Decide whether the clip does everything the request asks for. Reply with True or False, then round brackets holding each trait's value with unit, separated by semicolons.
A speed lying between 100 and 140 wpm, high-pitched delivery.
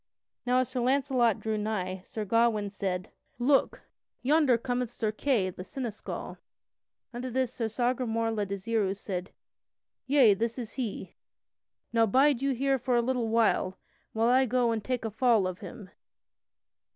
False (160 wpm; 230 Hz)